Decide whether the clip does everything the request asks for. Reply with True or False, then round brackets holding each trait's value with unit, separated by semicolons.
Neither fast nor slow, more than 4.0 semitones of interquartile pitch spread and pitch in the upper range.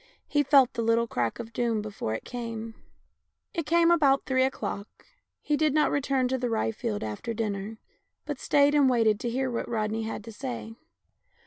False (190 wpm; 3.6 semitones; 235 Hz)